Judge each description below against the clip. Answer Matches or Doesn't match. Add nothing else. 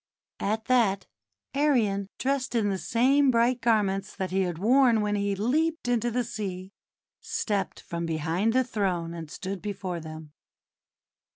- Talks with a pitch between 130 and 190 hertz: Doesn't match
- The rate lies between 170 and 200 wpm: Doesn't match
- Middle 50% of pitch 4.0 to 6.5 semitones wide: Matches